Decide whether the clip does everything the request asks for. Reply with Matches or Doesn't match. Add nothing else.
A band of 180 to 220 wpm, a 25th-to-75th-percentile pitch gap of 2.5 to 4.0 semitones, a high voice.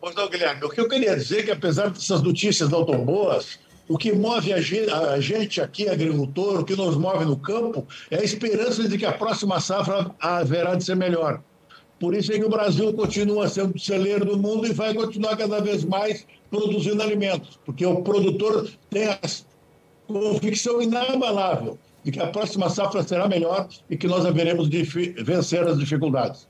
Matches